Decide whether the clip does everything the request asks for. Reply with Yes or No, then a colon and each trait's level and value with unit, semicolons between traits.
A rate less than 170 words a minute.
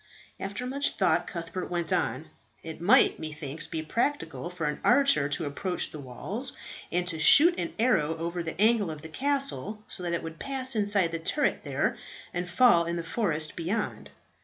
No: average, 185 wpm